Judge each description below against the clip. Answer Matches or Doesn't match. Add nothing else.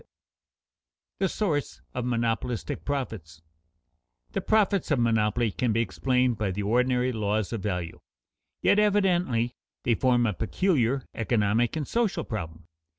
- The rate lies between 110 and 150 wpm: Matches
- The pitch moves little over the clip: Doesn't match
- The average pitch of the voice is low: Matches